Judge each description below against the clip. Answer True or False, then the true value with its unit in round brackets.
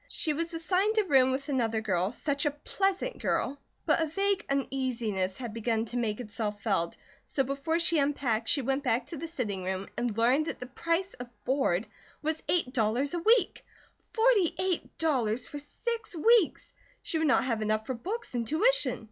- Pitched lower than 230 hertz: False (275 Hz)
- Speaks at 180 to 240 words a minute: True (190 wpm)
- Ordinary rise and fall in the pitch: False (6.5 semitones)